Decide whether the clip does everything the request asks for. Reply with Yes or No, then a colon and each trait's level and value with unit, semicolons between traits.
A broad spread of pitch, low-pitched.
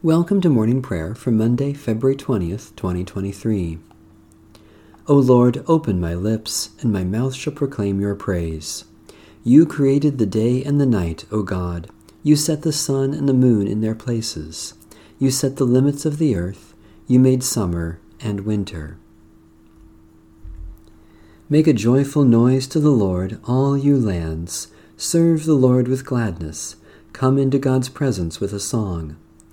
Yes: wide, 7.7 semitones; low, 110 Hz